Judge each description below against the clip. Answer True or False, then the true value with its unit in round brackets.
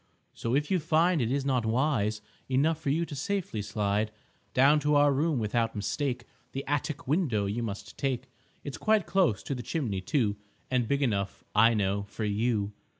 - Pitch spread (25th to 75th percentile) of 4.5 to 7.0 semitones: True (5.5 semitones)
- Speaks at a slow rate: False (185 wpm)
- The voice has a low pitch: True (130 Hz)